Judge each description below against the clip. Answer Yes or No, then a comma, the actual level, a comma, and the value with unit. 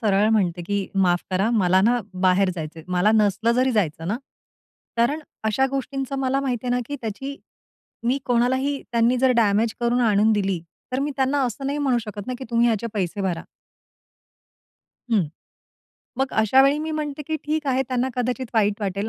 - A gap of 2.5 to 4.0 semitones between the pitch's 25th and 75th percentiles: No, average, 4.8 semitones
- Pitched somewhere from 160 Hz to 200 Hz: No, high, 235 Hz